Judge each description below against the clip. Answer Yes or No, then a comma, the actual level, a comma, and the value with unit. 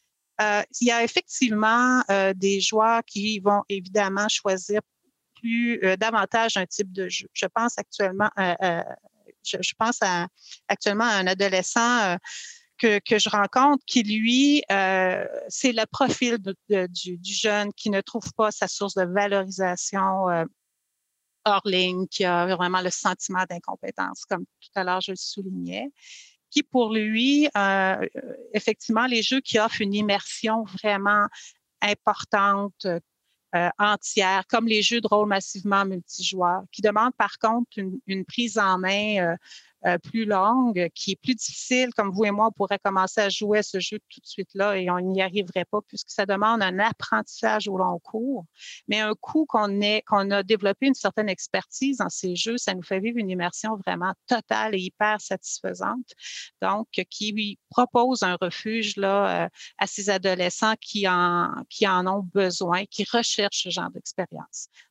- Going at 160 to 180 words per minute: Yes, average, 165 wpm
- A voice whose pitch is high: Yes, high, 205 Hz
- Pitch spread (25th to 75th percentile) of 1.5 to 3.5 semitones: Yes, average, 2.8 semitones